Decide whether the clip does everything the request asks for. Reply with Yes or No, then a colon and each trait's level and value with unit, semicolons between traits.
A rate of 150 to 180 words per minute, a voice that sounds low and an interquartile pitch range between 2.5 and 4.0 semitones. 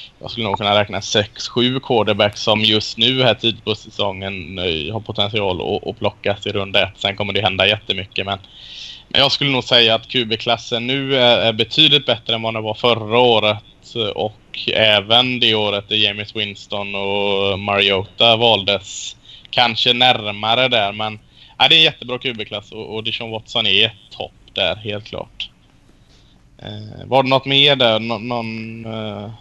Yes: average, 170 wpm; low, 110 Hz; average, 2.9 semitones